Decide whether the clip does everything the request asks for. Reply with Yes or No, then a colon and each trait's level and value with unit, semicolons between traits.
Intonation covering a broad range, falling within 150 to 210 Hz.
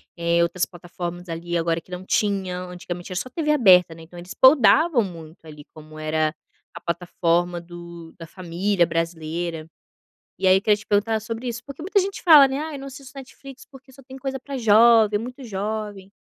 Yes: wide, 6.7 semitones; high, 190 Hz